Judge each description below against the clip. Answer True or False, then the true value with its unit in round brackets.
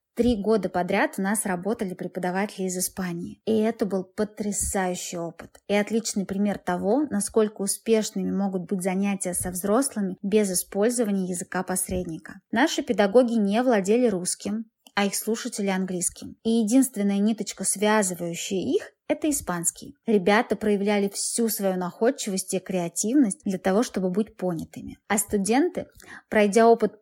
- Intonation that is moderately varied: True (3.1 semitones)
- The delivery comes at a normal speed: True (135 wpm)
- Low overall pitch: False (205 Hz)